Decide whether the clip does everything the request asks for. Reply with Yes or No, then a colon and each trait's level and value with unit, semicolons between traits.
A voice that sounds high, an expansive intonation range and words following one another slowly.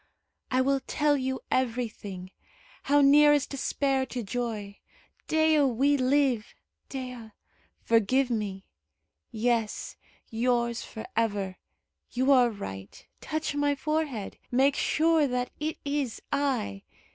No: very high, 255 Hz; average, 4.0 semitones; slow, 115 wpm